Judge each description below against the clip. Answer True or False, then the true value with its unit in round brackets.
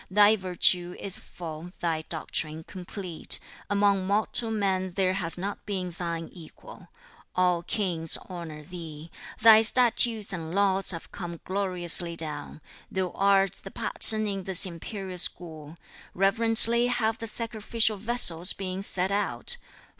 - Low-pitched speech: False (190 Hz)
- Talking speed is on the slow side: True (130 wpm)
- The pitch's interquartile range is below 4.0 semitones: True (3.1 semitones)